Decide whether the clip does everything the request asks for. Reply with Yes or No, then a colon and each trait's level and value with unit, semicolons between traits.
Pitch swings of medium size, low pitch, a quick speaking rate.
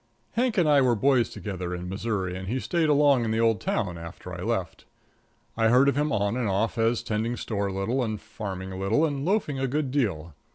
No: wide, 6.0 semitones; low, 115 Hz; fast, 230 wpm